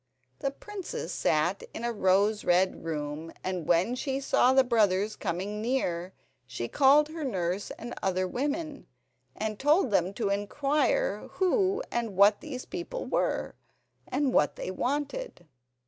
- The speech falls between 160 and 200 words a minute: No, average, 145 wpm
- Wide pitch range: Yes, wide, 7.6 semitones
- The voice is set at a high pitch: Yes, high, 230 Hz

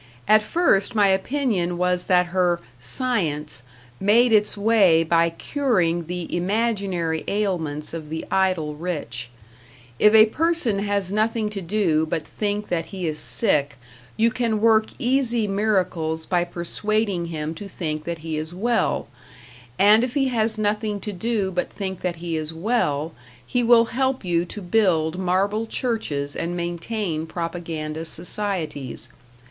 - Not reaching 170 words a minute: Yes, average, 145 wpm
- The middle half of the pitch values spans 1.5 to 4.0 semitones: No, average, 4.7 semitones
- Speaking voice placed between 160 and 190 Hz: Yes, medium, 185 Hz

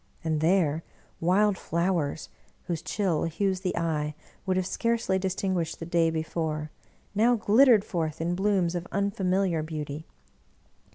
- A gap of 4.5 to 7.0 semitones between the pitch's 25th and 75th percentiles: No, average, 3.2 semitones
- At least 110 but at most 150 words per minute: Yes, average, 145 wpm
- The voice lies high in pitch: No, medium, 175 Hz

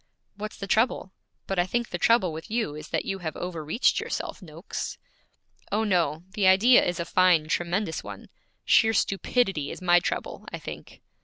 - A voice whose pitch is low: No, medium, 185 Hz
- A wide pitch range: No, average, 4.3 semitones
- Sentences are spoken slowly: No, average, 175 wpm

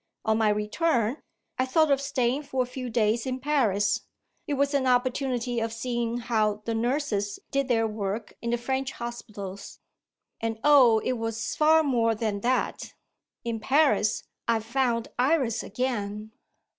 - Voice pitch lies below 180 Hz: No, high, 240 Hz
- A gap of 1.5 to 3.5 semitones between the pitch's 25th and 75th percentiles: Yes, average, 3.1 semitones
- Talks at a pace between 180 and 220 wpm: No, average, 155 wpm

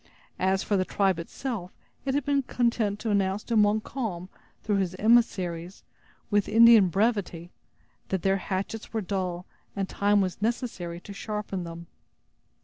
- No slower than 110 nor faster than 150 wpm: Yes, average, 145 wpm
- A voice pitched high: Yes, high, 200 Hz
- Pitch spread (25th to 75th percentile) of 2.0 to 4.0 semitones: Yes, average, 3.2 semitones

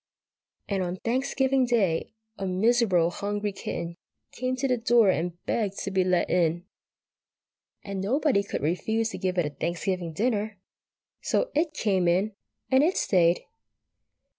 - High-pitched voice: Yes, high, 200 Hz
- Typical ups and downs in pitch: Yes, average, 5.0 semitones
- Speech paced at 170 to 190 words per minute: No, average, 145 wpm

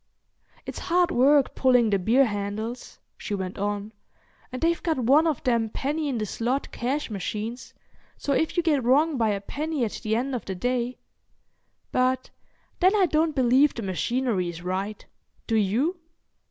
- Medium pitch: No, high, 245 Hz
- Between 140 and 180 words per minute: Yes, average, 165 wpm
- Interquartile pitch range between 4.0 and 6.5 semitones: Yes, average, 5.3 semitones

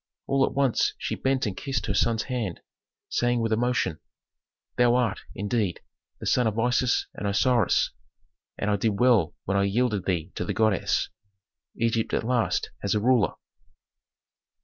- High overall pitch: No, low, 115 Hz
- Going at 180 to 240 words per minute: No, average, 160 wpm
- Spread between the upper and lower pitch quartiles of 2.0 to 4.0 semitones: Yes, average, 3.3 semitones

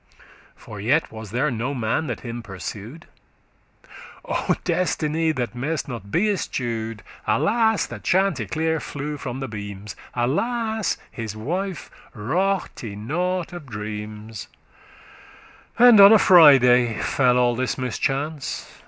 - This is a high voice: No, low, 130 Hz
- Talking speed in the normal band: No, slow, 125 wpm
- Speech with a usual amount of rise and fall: No, wide, 6.8 semitones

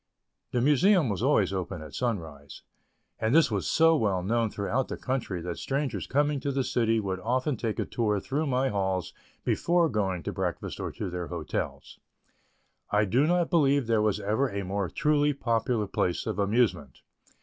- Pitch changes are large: Yes, wide, 6.1 semitones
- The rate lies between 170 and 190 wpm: Yes, average, 180 wpm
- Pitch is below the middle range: Yes, low, 115 Hz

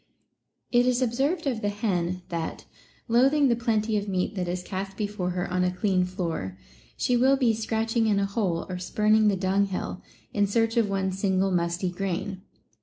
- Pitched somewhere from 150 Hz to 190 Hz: No, high, 200 Hz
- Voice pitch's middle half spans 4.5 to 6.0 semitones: No, average, 3.7 semitones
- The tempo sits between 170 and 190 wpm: Yes, average, 180 wpm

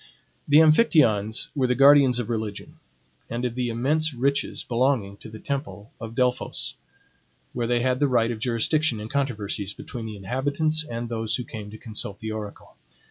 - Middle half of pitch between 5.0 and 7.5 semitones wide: No, average, 3.9 semitones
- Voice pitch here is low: Yes, low, 120 Hz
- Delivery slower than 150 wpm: No, average, 175 wpm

